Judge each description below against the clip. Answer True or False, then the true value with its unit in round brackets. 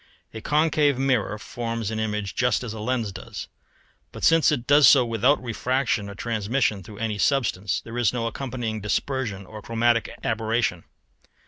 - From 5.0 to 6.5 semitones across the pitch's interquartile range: False (3.2 semitones)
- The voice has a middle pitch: False (115 Hz)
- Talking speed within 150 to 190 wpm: True (160 wpm)